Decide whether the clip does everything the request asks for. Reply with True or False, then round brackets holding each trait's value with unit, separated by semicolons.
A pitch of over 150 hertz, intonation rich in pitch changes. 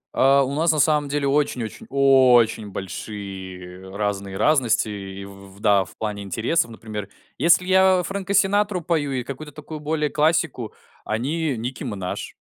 False (130 Hz; 7.2 semitones)